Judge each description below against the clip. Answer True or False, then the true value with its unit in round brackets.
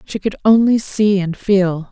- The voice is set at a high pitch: True (200 Hz)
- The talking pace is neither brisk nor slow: True (190 wpm)